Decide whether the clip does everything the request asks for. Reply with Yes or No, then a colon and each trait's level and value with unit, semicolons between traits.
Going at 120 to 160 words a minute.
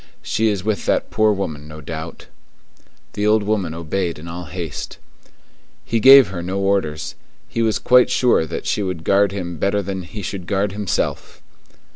No: average, 175 wpm